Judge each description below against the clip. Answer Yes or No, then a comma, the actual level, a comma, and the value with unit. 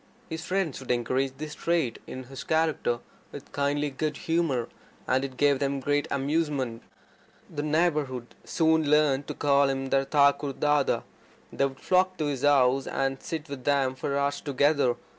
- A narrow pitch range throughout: Yes, narrow, 2.2 semitones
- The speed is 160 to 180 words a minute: Yes, average, 170 wpm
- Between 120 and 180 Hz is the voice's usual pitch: Yes, medium, 140 Hz